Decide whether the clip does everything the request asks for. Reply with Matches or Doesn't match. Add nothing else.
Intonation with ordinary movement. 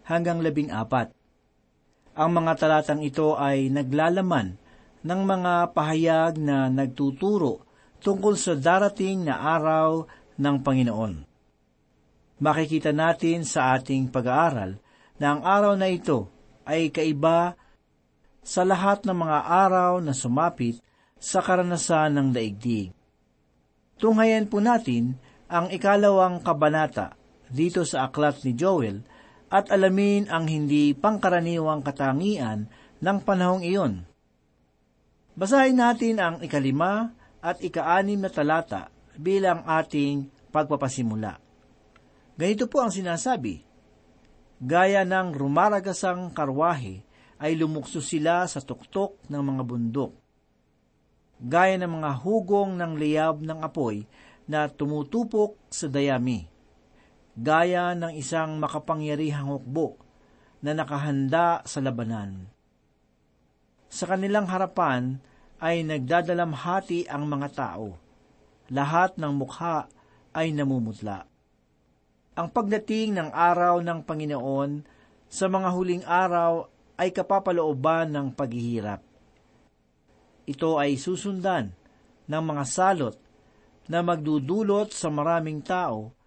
Matches